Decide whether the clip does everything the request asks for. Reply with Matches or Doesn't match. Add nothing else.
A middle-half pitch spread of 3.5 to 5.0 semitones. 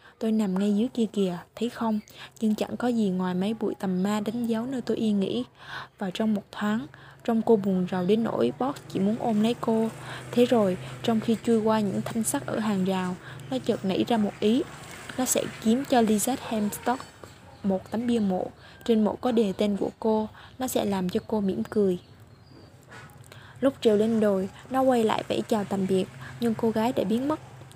Doesn't match